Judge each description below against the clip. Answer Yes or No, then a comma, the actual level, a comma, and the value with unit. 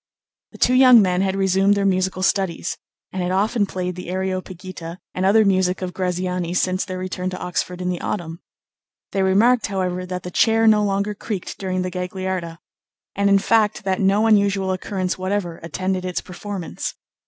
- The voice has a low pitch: No, medium, 185 Hz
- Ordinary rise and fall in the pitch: No, narrow, 1.6 semitones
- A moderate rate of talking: Yes, average, 175 wpm